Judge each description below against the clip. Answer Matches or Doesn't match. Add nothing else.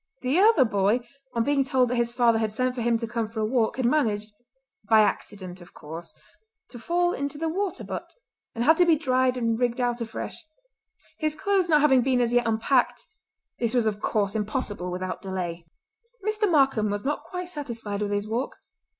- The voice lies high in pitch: Matches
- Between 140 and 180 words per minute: Doesn't match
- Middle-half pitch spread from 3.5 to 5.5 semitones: Matches